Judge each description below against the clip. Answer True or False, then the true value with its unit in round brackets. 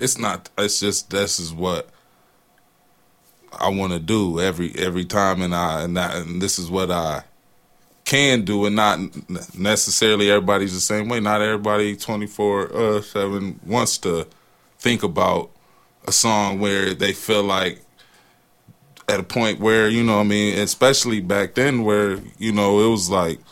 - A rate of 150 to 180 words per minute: True (165 wpm)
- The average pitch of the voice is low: True (100 Hz)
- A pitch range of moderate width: False (2.1 semitones)